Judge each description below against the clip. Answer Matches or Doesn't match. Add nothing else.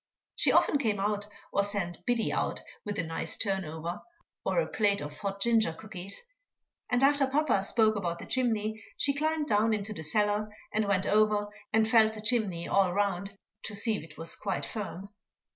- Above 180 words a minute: Matches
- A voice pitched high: Matches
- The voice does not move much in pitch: Matches